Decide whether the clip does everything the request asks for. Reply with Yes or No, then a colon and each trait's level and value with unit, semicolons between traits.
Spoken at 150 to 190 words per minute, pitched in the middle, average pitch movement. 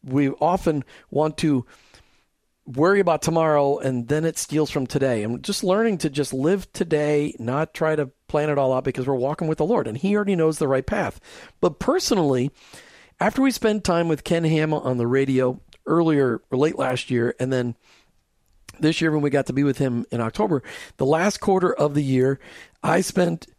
No: average, 200 wpm; medium, 150 Hz; average, 3.9 semitones